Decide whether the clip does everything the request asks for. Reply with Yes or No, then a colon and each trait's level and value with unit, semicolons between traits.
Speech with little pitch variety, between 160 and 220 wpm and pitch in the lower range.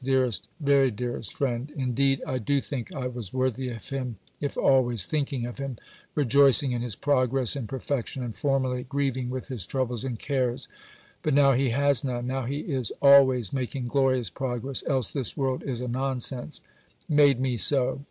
Yes: narrow, 2.1 semitones; average, 175 wpm; low, 130 Hz